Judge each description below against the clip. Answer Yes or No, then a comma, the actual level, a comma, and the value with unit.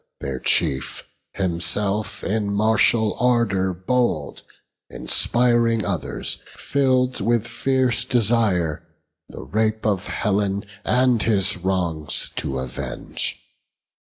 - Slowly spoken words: Yes, slow, 95 wpm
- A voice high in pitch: No, low, 105 Hz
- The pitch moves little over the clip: No, average, 4.2 semitones